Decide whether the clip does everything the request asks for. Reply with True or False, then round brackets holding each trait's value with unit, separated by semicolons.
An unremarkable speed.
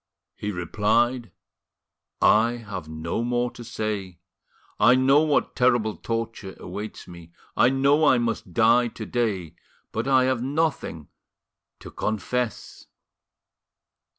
False (120 wpm)